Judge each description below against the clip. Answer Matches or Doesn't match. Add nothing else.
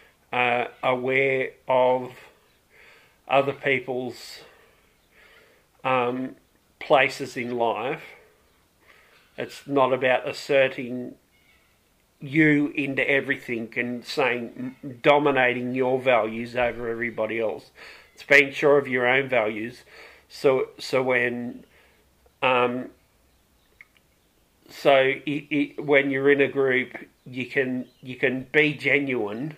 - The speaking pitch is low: Matches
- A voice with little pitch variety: Matches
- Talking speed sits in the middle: Doesn't match